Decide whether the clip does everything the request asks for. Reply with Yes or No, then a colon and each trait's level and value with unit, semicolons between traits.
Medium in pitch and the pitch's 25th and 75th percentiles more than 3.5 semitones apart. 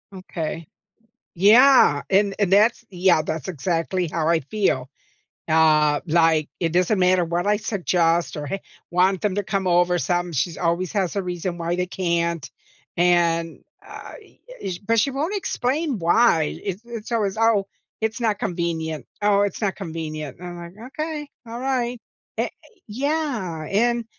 Yes: medium, 180 Hz; average, 4.3 semitones